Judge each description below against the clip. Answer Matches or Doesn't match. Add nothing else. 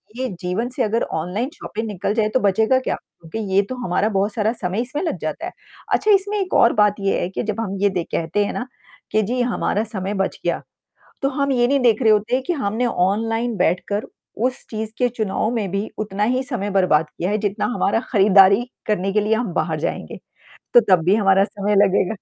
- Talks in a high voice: Matches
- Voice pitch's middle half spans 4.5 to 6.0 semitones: Doesn't match